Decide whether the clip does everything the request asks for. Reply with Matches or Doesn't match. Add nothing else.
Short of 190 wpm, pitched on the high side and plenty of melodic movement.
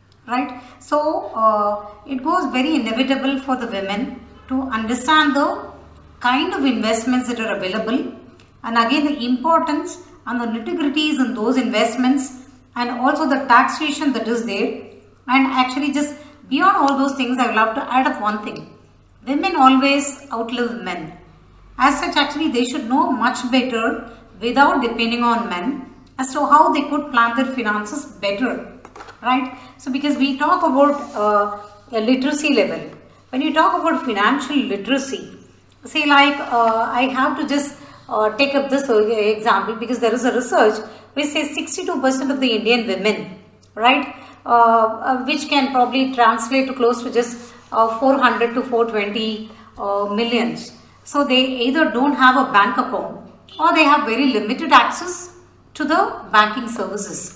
Doesn't match